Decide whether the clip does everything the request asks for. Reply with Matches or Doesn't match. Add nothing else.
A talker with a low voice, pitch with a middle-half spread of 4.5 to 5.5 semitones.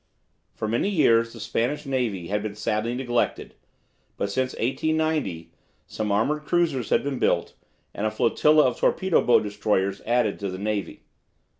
Matches